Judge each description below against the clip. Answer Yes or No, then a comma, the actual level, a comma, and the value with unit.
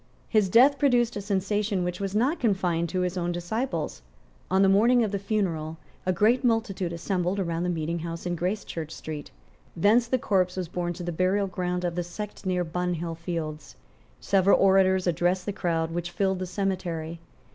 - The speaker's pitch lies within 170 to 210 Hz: Yes, medium, 185 Hz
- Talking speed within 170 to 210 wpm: Yes, average, 185 wpm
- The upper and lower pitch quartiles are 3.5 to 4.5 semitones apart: No, average, 2.8 semitones